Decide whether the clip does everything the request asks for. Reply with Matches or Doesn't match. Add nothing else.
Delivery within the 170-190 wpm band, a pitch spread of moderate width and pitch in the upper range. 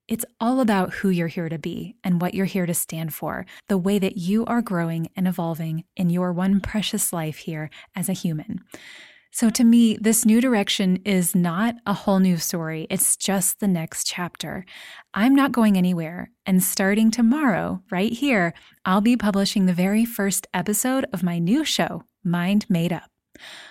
Matches